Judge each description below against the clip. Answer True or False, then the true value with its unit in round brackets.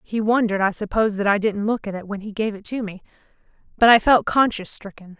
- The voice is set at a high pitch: True (210 Hz)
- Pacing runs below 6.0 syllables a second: False (6.5 syllables/s)